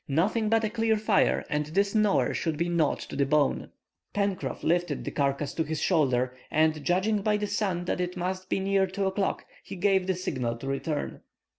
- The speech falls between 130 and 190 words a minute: No, average, 200 wpm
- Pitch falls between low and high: Yes, medium, 180 Hz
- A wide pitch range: No, average, 4.7 semitones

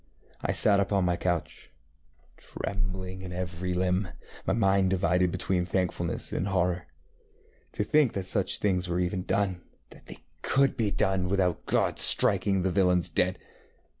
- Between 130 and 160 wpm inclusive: Yes, average, 150 wpm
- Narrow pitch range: Yes, narrow, 1.5 semitones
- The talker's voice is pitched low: Yes, very low, 95 Hz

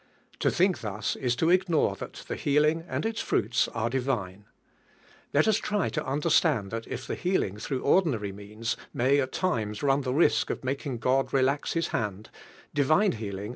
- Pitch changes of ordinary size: No, wide, 6.1 semitones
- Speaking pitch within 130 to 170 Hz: Yes, low, 135 Hz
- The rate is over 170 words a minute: Yes, average, 185 wpm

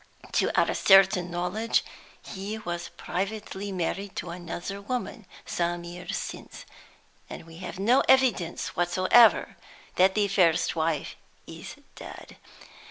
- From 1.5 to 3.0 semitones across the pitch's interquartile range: Yes, average, 2.7 semitones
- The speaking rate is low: Yes, slow, 120 wpm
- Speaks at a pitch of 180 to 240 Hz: Yes, medium, 185 Hz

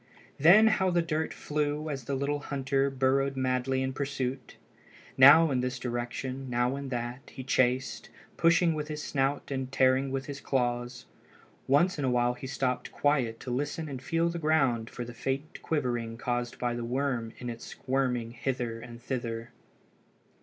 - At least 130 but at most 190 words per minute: Yes, average, 170 wpm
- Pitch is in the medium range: No, low, 130 Hz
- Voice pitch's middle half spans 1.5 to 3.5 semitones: Yes, average, 2.7 semitones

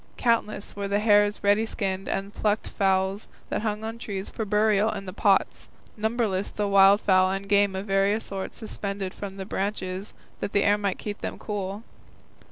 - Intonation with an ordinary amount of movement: No, narrow, 1.4 semitones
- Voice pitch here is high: Yes, high, 200 Hz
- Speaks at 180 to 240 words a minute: Yes, average, 185 wpm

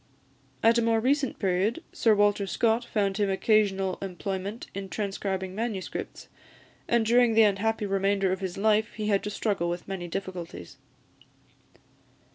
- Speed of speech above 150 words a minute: No, average, 145 wpm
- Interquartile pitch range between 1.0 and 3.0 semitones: Yes, narrow, 2.6 semitones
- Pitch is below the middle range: No, high, 200 Hz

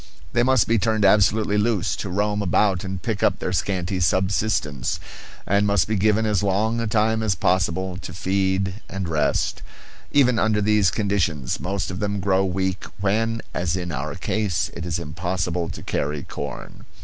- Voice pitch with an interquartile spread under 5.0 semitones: Yes, average, 3.0 semitones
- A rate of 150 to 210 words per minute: Yes, average, 175 wpm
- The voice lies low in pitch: Yes, very low, 95 Hz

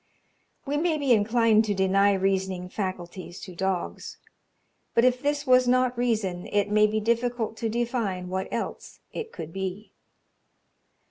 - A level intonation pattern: No, average, 4.3 semitones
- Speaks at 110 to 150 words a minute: Yes, average, 145 wpm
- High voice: Yes, high, 215 Hz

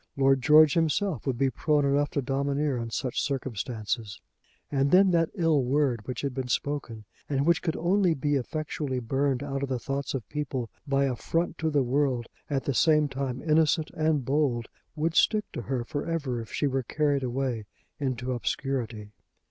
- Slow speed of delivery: No, average, 185 wpm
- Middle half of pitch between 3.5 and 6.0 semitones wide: No, average, 3.1 semitones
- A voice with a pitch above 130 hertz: Yes, medium, 140 Hz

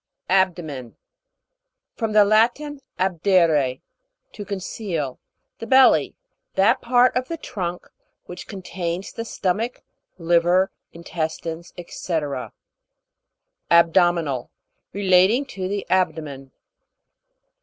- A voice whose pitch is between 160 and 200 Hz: Yes, medium, 185 Hz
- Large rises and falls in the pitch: No, average, 4.0 semitones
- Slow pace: Yes, slow, 90 wpm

